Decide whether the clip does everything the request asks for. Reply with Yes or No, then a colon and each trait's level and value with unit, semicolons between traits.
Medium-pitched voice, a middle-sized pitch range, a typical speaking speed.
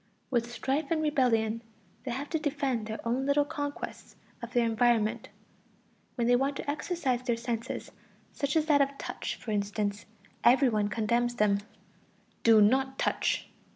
No: high, 245 Hz; average, 3.7 semitones; average, 155 wpm